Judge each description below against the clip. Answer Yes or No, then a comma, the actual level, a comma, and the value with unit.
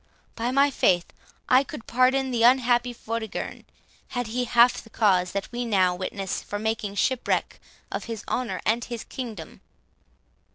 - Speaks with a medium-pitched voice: No, high, 230 Hz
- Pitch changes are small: No, average, 3.3 semitones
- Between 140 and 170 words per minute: Yes, average, 155 wpm